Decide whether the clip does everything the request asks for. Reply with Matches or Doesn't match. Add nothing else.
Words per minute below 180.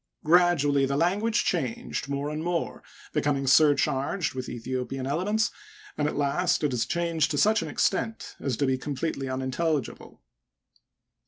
Matches